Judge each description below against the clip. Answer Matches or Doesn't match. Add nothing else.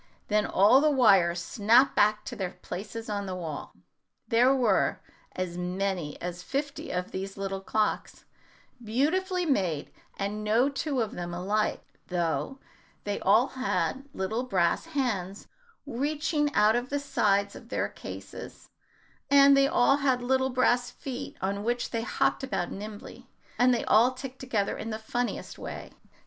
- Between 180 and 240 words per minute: Doesn't match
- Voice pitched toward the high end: Matches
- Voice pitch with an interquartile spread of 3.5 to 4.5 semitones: Doesn't match